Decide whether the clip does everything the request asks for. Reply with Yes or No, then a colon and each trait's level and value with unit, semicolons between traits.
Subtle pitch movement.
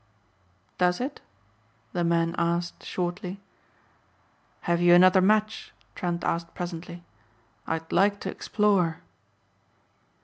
Yes: narrow, 1.9 semitones